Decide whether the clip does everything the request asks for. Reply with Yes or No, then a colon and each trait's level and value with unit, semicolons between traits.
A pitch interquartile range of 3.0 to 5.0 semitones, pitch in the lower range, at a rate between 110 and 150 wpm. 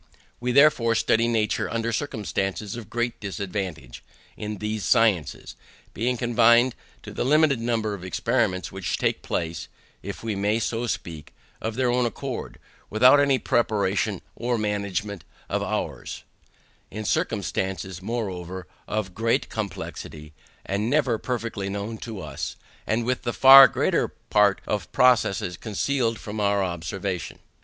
Yes: average, 3.4 semitones; low, 110 Hz; average, 140 wpm